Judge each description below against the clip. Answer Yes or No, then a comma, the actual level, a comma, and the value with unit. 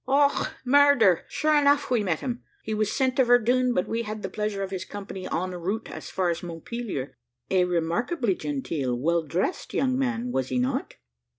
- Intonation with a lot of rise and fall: Yes, wide, 6.5 semitones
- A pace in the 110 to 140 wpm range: No, average, 190 wpm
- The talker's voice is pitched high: Yes, high, 210 Hz